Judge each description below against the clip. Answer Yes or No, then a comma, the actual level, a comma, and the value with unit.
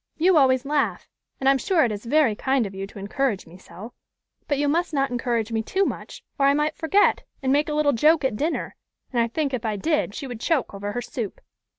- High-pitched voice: Yes, very high, 270 Hz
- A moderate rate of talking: No, fast, 245 wpm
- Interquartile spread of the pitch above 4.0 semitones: Yes, average, 5.0 semitones